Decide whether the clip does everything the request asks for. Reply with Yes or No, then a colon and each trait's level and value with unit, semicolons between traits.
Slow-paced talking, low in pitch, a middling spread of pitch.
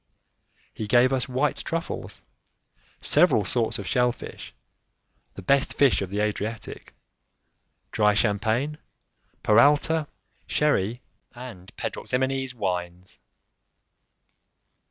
Yes: slow, 95 wpm; low, 120 Hz; average, 4.3 semitones